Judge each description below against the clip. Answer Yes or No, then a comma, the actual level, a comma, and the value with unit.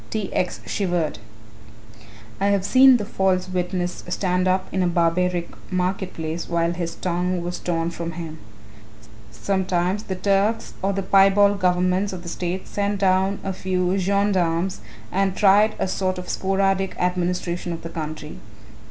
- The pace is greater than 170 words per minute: No, average, 150 wpm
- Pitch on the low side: No, medium, 185 Hz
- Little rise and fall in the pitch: Yes, narrow, 1.8 semitones